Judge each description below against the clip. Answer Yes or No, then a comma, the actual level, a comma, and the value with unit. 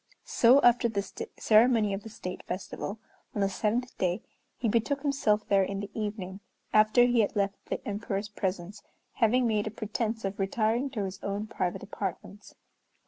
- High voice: Yes, high, 210 Hz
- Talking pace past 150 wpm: Yes, average, 170 wpm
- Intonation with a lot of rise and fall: No, narrow, 2.6 semitones